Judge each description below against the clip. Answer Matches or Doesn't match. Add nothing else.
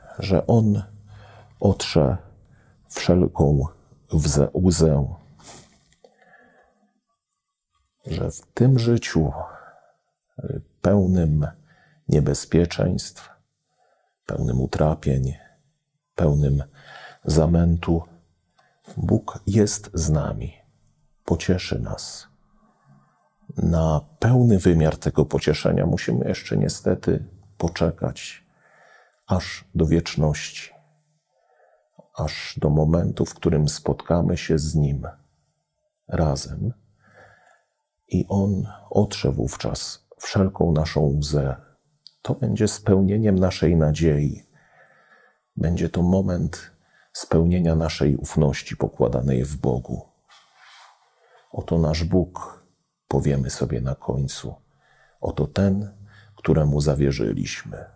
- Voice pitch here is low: Matches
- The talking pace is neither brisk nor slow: Doesn't match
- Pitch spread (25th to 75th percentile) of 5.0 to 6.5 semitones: Matches